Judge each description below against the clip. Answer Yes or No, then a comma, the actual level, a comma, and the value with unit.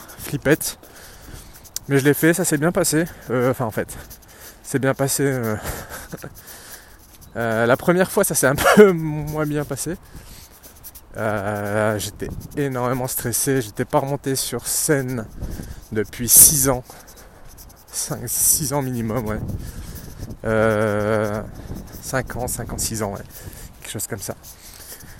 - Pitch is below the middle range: Yes, low, 120 Hz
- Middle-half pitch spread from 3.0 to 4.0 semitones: No, average, 4.9 semitones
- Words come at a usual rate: No, slow, 125 wpm